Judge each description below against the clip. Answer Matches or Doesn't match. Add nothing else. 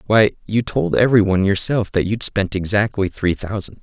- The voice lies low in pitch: Matches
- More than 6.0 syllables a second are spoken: Doesn't match